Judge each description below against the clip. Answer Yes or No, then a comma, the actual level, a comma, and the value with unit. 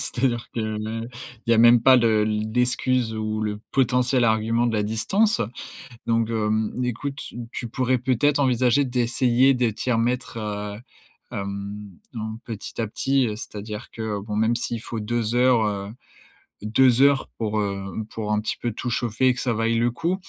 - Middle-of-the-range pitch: No, low, 115 Hz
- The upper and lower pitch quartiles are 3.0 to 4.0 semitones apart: No, narrow, 2.5 semitones